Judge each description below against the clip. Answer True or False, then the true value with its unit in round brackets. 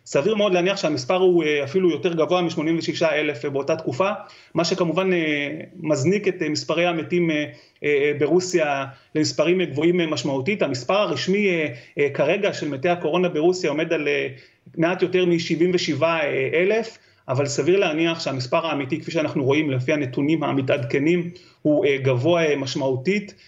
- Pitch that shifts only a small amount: False (3.3 semitones)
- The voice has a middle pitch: True (165 Hz)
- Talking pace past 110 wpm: True (130 wpm)